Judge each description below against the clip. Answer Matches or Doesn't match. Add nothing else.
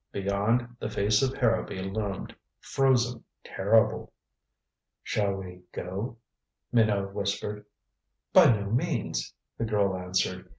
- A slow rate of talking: Matches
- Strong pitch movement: Doesn't match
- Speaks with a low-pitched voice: Matches